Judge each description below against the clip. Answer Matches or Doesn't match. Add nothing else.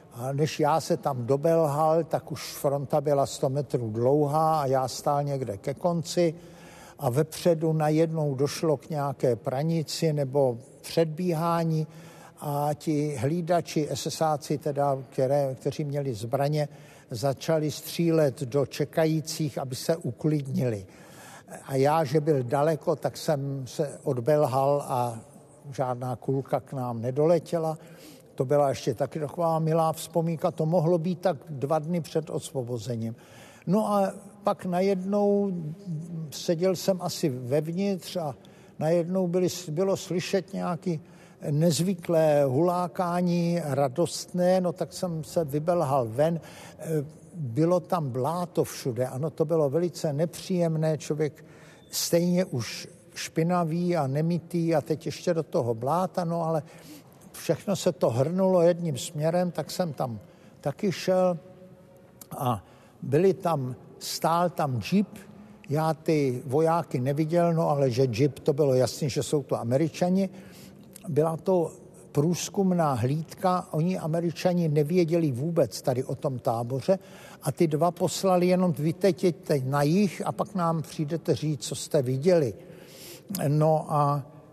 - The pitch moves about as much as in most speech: Matches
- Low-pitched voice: Doesn't match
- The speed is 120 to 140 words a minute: Matches